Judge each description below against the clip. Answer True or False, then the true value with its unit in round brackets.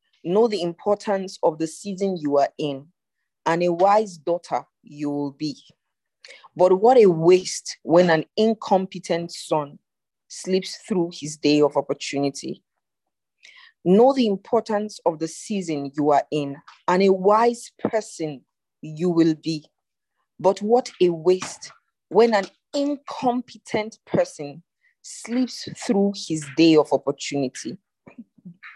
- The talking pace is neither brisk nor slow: False (125 wpm)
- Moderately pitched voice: True (180 Hz)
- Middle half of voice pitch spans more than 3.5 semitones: True (5.1 semitones)